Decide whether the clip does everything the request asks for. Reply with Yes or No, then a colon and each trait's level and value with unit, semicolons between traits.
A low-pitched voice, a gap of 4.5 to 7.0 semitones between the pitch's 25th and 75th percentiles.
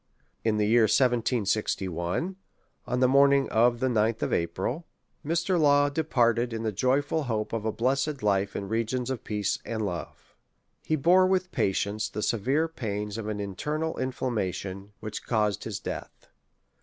Yes: low, 115 Hz; average, 4.9 semitones